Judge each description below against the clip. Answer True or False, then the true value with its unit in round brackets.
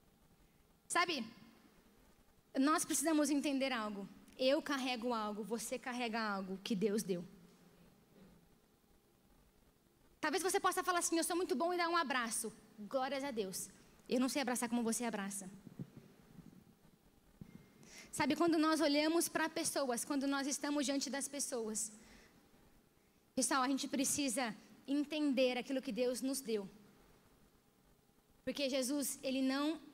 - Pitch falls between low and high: False (260 Hz)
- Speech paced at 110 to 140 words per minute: True (125 wpm)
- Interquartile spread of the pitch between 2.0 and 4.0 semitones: False (5.1 semitones)